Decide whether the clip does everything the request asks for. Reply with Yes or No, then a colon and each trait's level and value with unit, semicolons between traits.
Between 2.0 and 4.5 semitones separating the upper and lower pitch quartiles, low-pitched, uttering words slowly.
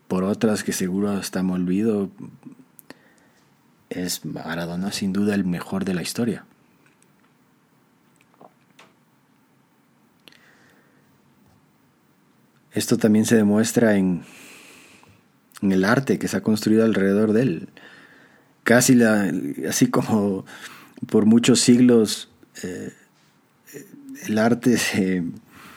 Yes: average, 2.9 semitones; low, 105 Hz; slow, 100 wpm